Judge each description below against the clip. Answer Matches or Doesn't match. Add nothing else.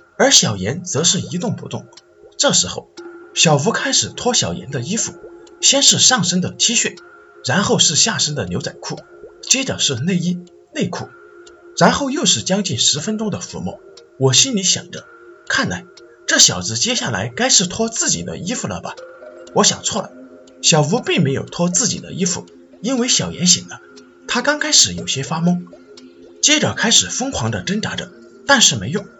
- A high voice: Matches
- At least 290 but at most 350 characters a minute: Doesn't match